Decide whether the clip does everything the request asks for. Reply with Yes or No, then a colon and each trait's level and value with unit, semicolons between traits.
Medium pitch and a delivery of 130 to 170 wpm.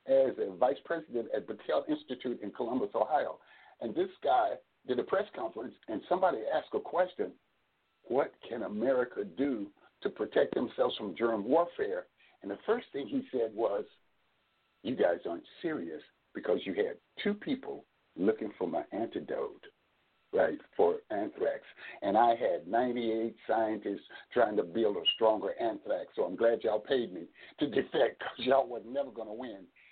No: very high, 335 Hz; average, 160 wpm